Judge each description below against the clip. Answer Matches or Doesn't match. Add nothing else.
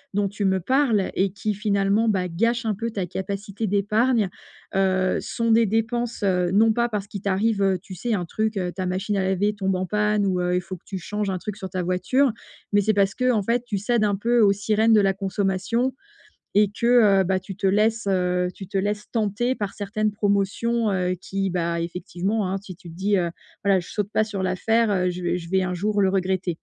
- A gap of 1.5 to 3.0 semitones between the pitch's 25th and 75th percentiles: Matches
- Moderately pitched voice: Doesn't match